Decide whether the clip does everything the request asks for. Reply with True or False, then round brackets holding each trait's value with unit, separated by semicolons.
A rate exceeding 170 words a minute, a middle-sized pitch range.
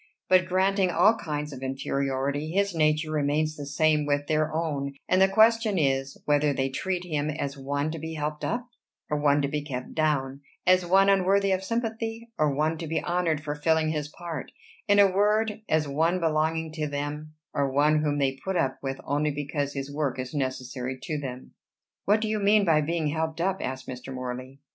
True (200 wpm; 4.0 semitones)